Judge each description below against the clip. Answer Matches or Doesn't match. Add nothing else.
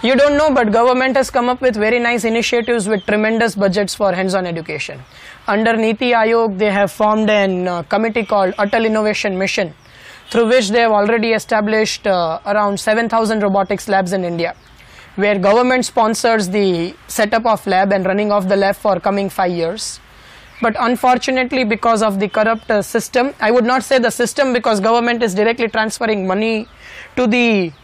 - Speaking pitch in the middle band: Doesn't match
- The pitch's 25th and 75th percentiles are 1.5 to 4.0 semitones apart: Matches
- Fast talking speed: Matches